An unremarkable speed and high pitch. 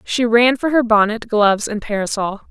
Yes: average, 190 wpm; high, 225 Hz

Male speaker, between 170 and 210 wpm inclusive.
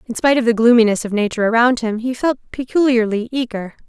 No: female; average, 200 wpm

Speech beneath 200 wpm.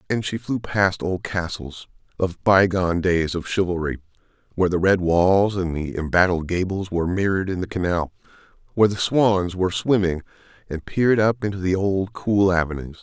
Yes: average, 175 wpm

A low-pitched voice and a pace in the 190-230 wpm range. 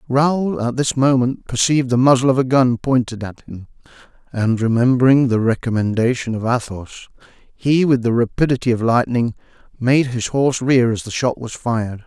No: low, 125 Hz; average, 170 wpm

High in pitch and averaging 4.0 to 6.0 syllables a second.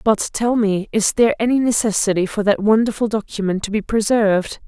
Yes: high, 215 Hz; 5.6 syllables/s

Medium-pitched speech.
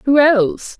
No: very high, 255 Hz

